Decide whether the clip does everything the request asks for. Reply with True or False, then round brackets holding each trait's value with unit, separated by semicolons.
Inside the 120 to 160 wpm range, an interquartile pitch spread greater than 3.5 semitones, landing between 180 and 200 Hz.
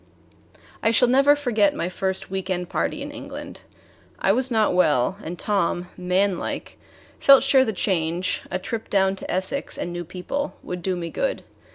False (175 wpm; 4.3 semitones; 190 Hz)